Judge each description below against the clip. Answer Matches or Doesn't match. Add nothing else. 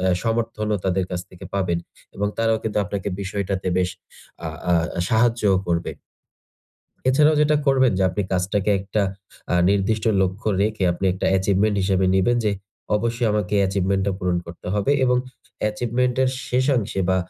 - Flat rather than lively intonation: Doesn't match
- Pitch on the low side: Matches